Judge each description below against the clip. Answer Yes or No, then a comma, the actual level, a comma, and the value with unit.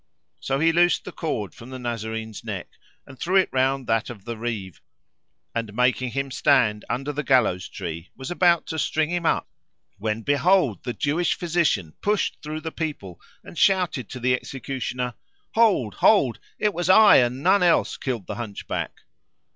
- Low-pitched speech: Yes, low, 130 Hz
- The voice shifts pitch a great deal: Yes, wide, 6.4 semitones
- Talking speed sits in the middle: Yes, average, 170 wpm